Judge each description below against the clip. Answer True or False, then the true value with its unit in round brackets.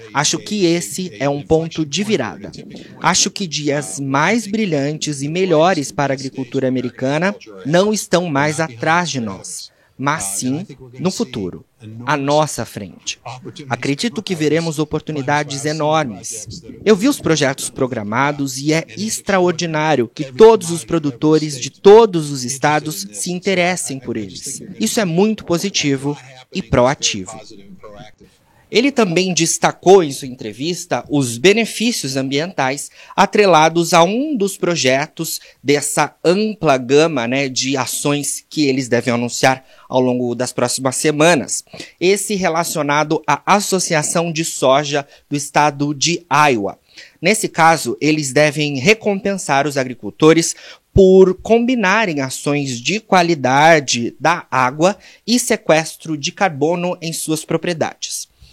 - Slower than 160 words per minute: True (125 wpm)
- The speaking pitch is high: False (155 Hz)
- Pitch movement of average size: True (4.7 semitones)